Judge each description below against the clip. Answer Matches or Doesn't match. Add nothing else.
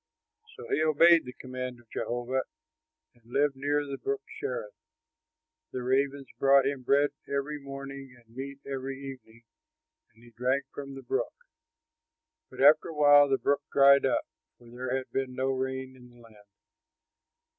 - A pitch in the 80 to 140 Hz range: Matches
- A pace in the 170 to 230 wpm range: Doesn't match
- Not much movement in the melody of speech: Matches